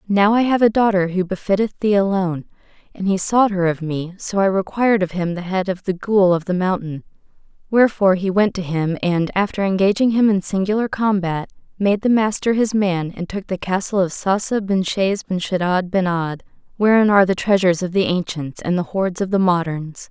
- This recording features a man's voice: No, female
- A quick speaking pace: Yes, fast, 210 wpm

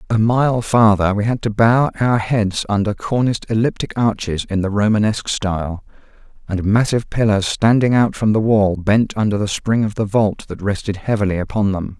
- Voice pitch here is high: No, low, 105 Hz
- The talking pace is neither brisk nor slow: Yes, average, 185 wpm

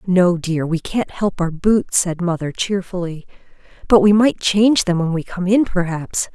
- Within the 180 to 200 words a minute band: Yes, average, 190 wpm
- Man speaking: No, female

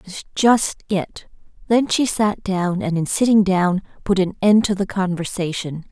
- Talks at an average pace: Yes, average, 185 wpm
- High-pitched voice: Yes, high, 195 Hz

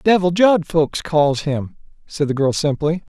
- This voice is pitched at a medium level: Yes, medium, 160 Hz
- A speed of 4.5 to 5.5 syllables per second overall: No, 4.1 syllables/s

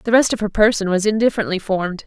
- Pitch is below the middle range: No, high, 205 Hz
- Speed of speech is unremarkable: No, fast, 235 wpm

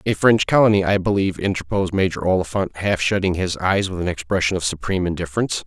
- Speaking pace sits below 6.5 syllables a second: No, 6.7 syllables/s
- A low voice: Yes, very low, 95 Hz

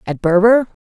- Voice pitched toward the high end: Yes, high, 200 Hz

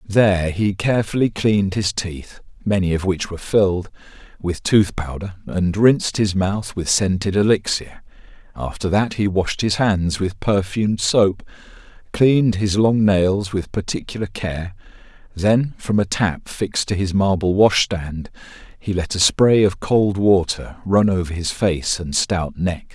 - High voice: No, very low, 95 Hz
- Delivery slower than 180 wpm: Yes, average, 155 wpm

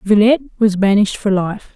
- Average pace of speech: Yes, average, 170 wpm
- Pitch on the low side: No, high, 210 Hz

